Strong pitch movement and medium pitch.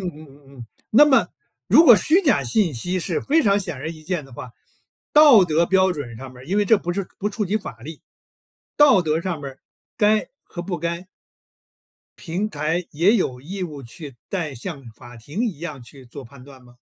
Yes: wide, 6.2 semitones; medium, 170 Hz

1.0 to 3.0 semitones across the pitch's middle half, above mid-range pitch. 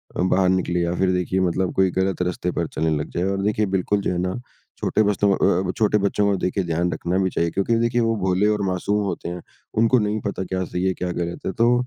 No: narrow, 2.5 semitones; very low, 95 Hz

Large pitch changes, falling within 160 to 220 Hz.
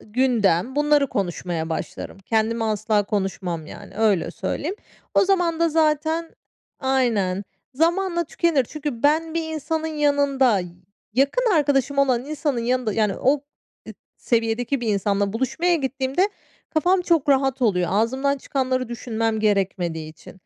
No: wide, 6.0 semitones; very high, 260 Hz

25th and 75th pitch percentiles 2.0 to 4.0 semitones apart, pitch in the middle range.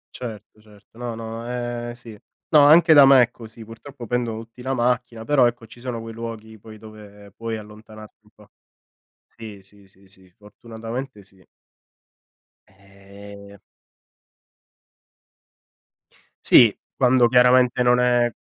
No: narrow, 2.6 semitones; low, 115 Hz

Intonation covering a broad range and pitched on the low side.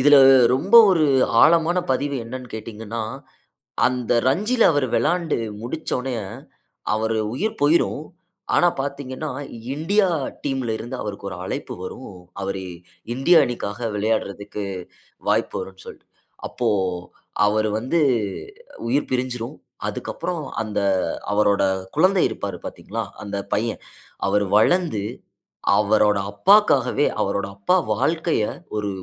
Yes: wide, 6.7 semitones; low, 125 Hz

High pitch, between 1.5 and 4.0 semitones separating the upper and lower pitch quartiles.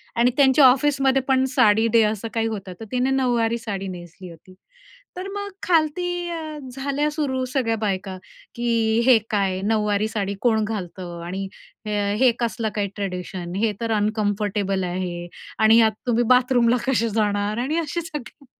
No: high, 225 Hz; average, 4.6 semitones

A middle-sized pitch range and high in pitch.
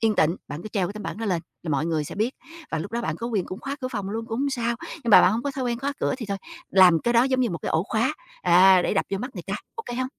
Yes: average, 4.8 semitones; high, 220 Hz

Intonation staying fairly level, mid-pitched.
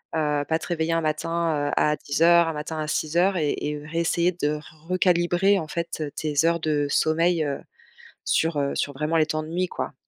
Yes: narrow, 2.1 semitones; medium, 160 Hz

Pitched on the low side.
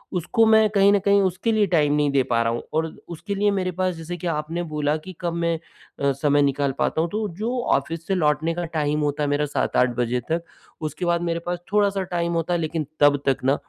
No: medium, 165 Hz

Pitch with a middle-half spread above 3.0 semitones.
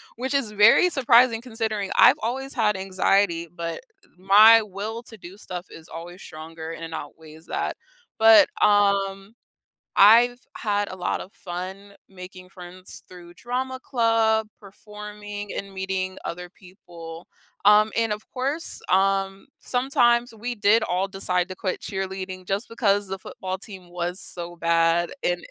Yes: average, 3.5 semitones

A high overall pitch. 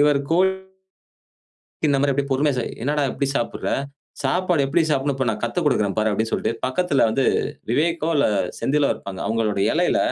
No: medium, 140 Hz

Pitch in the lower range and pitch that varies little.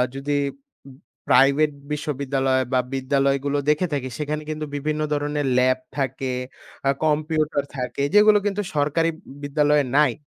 No: medium, 145 Hz; narrow, 1.9 semitones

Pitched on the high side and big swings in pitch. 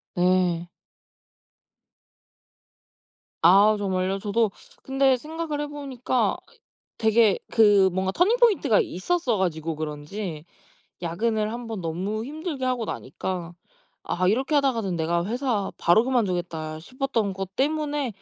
Yes: high, 215 Hz; wide, 6.3 semitones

